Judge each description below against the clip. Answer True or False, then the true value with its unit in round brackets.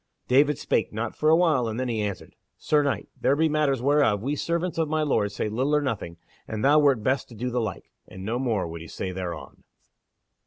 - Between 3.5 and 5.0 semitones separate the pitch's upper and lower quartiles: False (5.6 semitones)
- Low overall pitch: True (130 Hz)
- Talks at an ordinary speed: False (230 wpm)